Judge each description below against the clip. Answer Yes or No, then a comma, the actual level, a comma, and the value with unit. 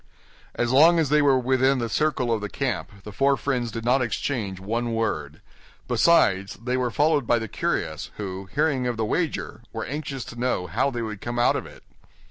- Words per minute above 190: Yes, fast, 205 wpm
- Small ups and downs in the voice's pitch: No, average, 3.9 semitones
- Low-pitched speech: Yes, low, 120 Hz